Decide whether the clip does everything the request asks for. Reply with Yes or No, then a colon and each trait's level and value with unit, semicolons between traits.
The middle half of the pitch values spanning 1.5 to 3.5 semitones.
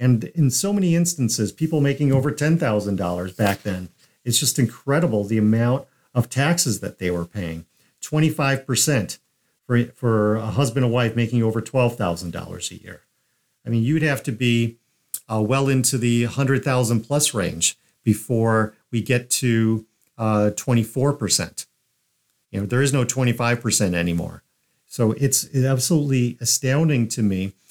No: average, 4.1 semitones